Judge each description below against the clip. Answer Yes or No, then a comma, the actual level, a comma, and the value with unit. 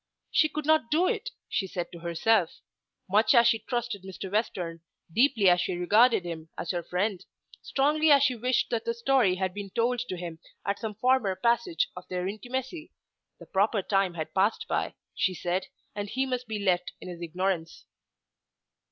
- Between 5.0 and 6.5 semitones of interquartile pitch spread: Yes, average, 5.3 semitones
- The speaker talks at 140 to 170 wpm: No, average, 185 wpm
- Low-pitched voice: No, high, 205 Hz